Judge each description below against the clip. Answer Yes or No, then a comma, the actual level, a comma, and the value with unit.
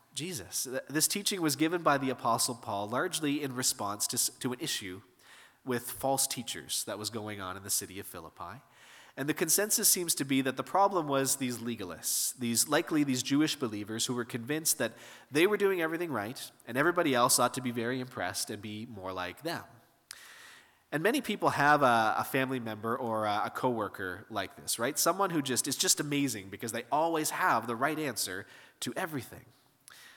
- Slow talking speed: No, average, 195 wpm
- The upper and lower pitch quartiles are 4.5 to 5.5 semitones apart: Yes, average, 5.2 semitones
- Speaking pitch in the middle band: No, low, 130 Hz